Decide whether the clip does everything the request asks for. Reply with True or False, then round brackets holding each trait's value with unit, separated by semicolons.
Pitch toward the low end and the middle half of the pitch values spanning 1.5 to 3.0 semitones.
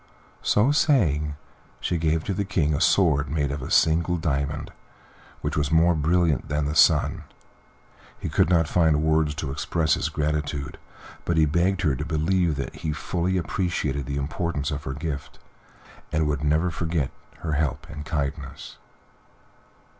True (75 Hz; 2.6 semitones)